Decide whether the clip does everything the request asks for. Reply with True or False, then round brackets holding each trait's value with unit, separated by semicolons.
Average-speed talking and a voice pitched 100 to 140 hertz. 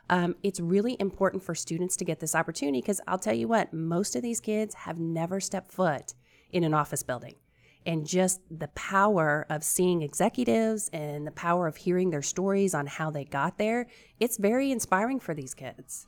False (195 wpm; 175 Hz)